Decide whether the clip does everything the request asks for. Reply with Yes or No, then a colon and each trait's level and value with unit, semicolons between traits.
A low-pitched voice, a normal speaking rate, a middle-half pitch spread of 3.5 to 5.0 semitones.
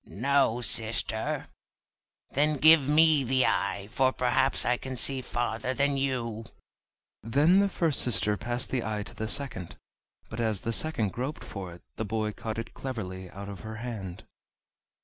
Yes: low, 120 Hz; average, 165 wpm; average, 4.0 semitones